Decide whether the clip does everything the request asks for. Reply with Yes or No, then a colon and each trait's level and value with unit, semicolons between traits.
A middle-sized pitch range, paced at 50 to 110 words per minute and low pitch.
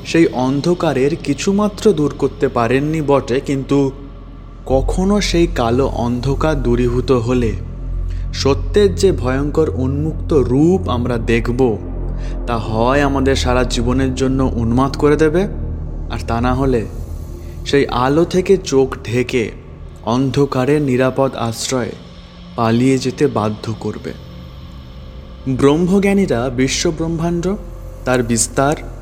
Yes: average, 4.2 semitones; average, 105 wpm; low, 130 Hz